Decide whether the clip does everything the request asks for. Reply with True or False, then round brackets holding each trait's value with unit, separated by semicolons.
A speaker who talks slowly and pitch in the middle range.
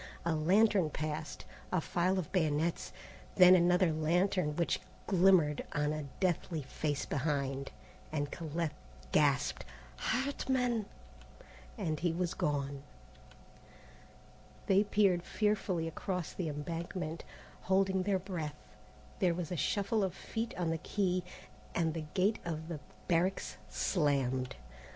True (120 wpm; 170 Hz)